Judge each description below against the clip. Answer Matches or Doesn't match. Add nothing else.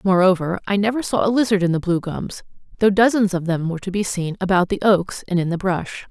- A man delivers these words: Doesn't match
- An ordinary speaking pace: Doesn't match